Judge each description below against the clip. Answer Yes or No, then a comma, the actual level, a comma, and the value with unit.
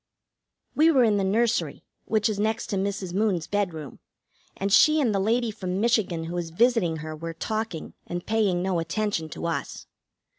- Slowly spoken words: No, average, 180 wpm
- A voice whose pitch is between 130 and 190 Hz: No, high, 200 Hz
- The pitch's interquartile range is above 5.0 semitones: No, average, 4.4 semitones